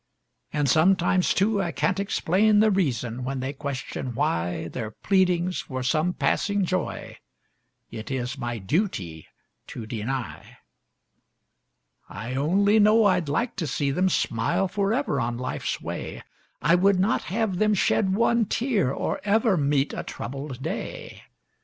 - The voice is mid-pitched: Yes, medium, 170 Hz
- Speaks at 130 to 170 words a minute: Yes, average, 140 wpm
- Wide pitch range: Yes, wide, 7.5 semitones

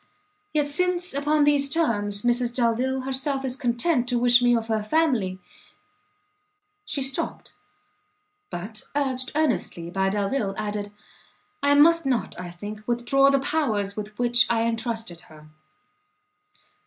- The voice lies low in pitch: No, high, 245 Hz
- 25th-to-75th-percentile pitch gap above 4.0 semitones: Yes, average, 5.2 semitones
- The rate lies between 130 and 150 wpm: Yes, slow, 135 wpm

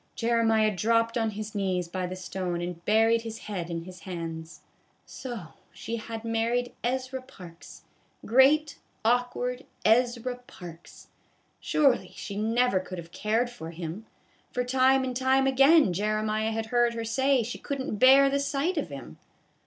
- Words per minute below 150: No, average, 155 wpm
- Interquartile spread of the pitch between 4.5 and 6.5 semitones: Yes, average, 5.1 semitones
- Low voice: No, high, 225 Hz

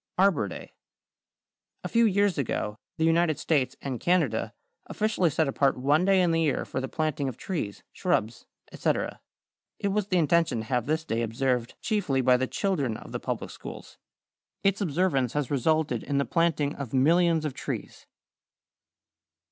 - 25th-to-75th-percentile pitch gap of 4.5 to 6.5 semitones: Yes, average, 5.2 semitones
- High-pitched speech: No, medium, 150 Hz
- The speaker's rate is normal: Yes, average, 165 wpm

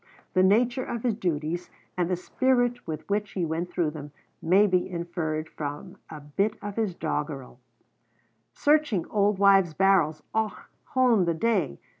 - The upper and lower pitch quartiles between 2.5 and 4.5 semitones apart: No, average, 4.9 semitones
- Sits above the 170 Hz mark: Yes, medium, 185 Hz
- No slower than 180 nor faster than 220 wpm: No, average, 155 wpm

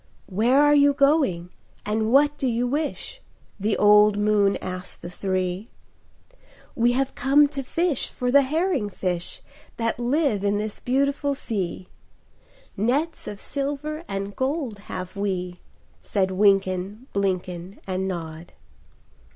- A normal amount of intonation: No, wide, 6.5 semitones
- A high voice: Yes, high, 215 Hz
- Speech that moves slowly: Yes, slow, 130 wpm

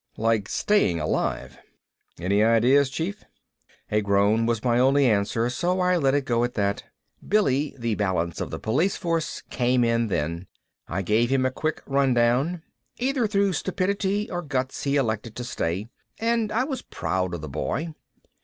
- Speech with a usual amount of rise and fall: No, wide, 7.8 semitones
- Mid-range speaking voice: No, low, 125 Hz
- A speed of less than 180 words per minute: Yes, average, 165 wpm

